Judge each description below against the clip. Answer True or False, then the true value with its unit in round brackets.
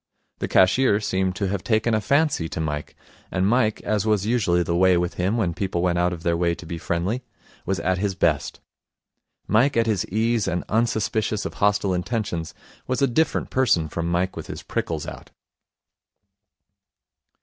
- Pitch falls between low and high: False (95 Hz)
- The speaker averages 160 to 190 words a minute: True (180 wpm)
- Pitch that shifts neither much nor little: True (4.0 semitones)